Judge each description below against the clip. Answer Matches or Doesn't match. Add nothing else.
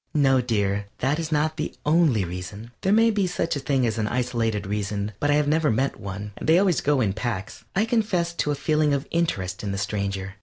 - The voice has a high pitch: Doesn't match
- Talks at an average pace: Doesn't match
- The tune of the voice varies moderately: Doesn't match